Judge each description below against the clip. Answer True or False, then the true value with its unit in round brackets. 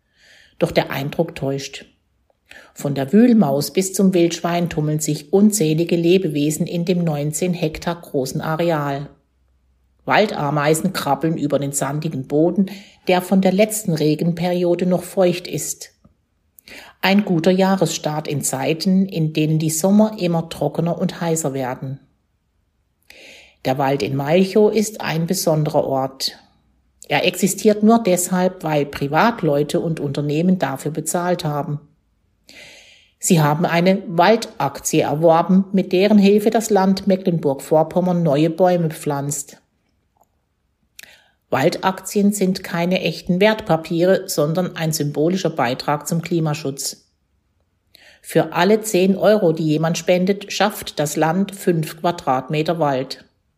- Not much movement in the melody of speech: False (4.2 semitones)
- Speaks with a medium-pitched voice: True (165 Hz)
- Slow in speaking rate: True (120 wpm)